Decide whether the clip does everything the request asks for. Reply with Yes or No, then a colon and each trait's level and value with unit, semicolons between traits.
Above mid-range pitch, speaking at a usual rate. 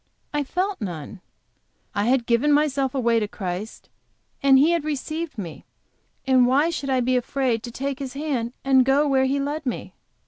Yes: very high, 265 Hz; average, 180 wpm